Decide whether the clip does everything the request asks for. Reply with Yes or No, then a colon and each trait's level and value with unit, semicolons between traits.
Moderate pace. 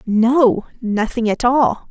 No: slow, 125 wpm